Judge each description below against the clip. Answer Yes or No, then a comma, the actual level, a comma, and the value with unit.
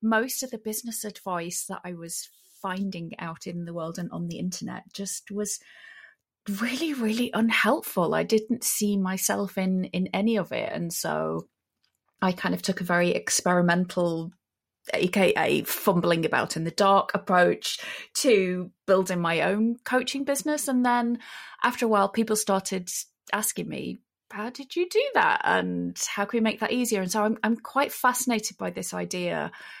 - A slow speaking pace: No, average, 165 wpm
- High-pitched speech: Yes, high, 200 Hz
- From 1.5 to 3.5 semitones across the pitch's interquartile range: No, average, 4.4 semitones